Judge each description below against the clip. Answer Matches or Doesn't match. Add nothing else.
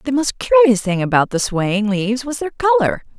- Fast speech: Matches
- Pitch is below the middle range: Doesn't match